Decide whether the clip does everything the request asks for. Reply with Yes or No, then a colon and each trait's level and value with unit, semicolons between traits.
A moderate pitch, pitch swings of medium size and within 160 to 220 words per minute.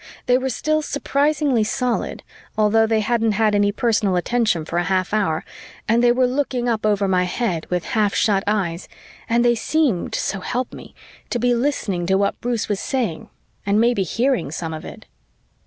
No: high, 220 Hz; average, 4.0 semitones; average, 185 wpm